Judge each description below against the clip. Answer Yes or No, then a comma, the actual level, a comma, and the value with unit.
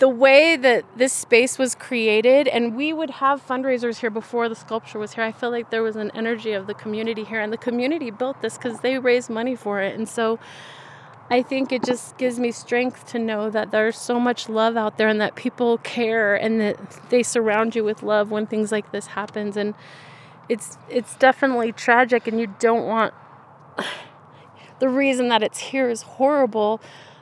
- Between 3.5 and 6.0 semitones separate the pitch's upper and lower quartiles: No, narrow, 2.6 semitones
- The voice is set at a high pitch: Yes, high, 230 Hz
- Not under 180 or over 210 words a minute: Yes, average, 200 wpm